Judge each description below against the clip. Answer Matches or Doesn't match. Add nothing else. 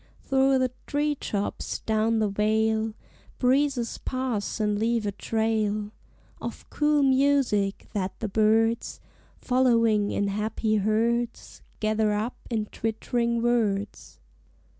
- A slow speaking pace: Matches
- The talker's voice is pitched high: Matches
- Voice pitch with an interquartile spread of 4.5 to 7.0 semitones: Doesn't match